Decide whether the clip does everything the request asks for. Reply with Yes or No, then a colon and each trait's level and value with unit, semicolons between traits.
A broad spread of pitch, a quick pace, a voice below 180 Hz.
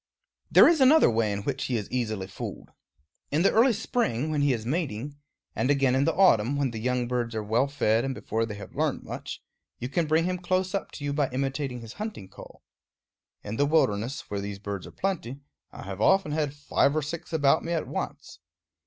Yes: wide, 5.8 semitones; fast, 215 wpm; low, 135 Hz